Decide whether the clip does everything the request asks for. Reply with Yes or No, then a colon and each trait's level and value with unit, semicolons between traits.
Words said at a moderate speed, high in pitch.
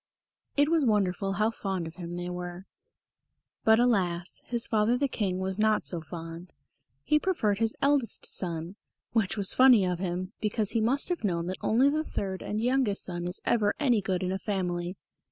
Yes: average, 190 wpm; high, 200 Hz